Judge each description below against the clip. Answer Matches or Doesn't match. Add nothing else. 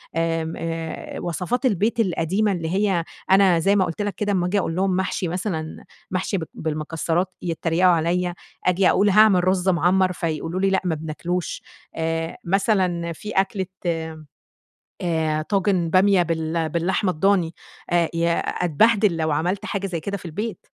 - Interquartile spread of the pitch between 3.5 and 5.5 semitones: Doesn't match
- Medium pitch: Matches